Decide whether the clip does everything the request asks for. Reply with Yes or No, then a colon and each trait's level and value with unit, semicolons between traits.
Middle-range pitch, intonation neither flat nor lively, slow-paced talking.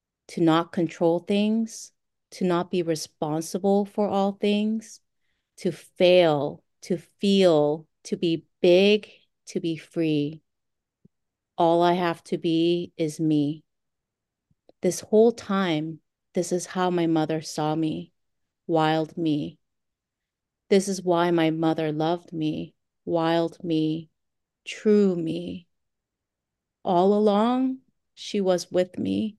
Yes: medium, 170 Hz; average, 3.6 semitones; slow, 115 wpm